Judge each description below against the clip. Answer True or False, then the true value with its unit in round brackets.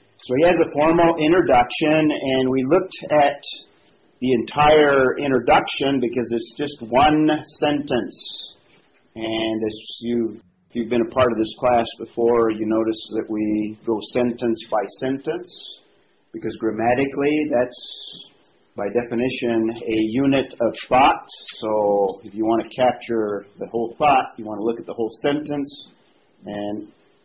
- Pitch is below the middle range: True (120 Hz)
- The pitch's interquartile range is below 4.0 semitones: False (4.3 semitones)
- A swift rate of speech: False (145 wpm)